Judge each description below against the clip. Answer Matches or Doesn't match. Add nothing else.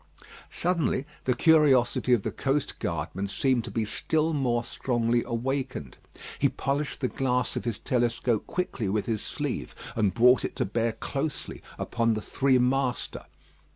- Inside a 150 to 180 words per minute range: Matches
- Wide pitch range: Doesn't match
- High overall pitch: Doesn't match